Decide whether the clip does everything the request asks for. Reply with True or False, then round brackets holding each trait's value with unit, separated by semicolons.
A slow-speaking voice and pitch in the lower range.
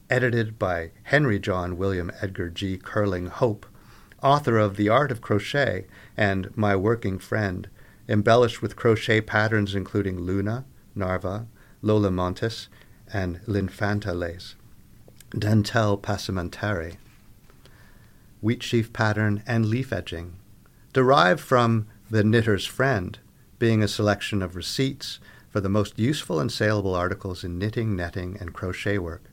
True (125 wpm; 105 Hz)